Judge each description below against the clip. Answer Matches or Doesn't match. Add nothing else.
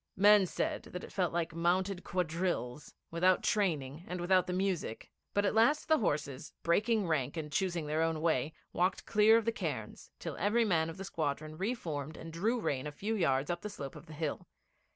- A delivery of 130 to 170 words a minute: Doesn't match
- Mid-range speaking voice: Matches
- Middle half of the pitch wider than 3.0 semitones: Matches